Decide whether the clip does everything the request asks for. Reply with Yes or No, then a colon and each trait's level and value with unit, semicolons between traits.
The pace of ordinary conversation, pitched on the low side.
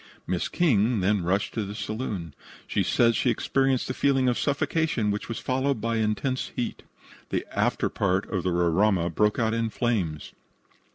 Yes: average, 165 wpm; low, 110 Hz